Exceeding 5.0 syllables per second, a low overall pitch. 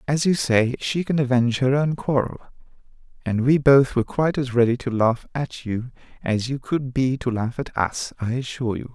Yes: 5.3 syllables/s; low, 130 Hz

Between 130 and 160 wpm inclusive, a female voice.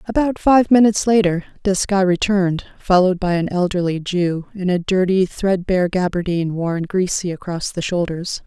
Yes: average, 150 wpm; female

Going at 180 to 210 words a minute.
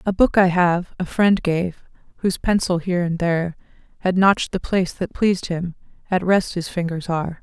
Yes: average, 195 wpm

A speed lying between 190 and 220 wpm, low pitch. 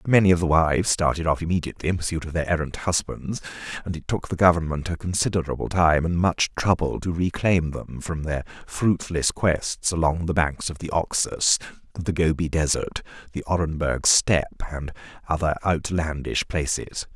No: average, 165 wpm; very low, 85 Hz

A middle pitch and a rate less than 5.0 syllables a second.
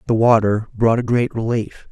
No: low, 115 Hz; 4.8 syllables/s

